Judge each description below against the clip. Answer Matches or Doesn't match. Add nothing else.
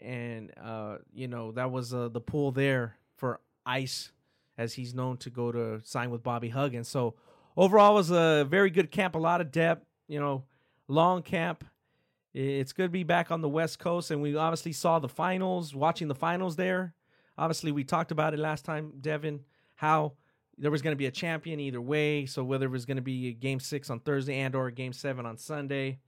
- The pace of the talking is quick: Matches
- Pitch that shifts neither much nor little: Matches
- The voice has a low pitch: Doesn't match